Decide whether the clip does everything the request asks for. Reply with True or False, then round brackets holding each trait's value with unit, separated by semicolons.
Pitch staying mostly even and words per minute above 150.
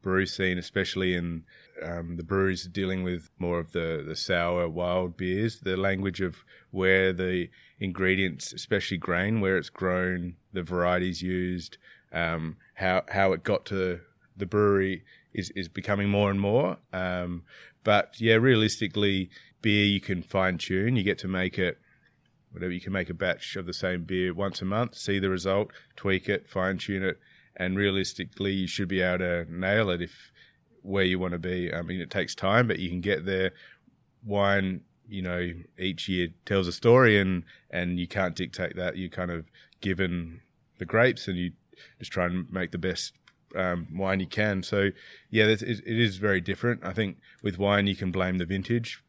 True (1.8 semitones; 185 wpm)